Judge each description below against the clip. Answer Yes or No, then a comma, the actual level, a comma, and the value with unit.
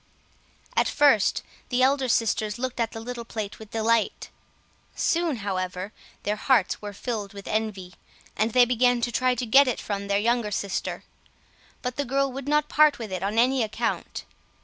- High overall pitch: Yes, high, 230 Hz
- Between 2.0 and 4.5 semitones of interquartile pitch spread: Yes, average, 3.6 semitones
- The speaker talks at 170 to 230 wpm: Yes, average, 175 wpm